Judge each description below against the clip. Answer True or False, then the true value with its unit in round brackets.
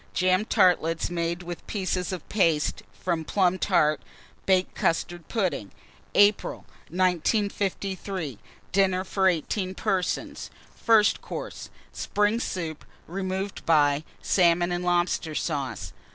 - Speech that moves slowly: True (110 wpm)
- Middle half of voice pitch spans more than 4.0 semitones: False (2.4 semitones)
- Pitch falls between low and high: True (180 Hz)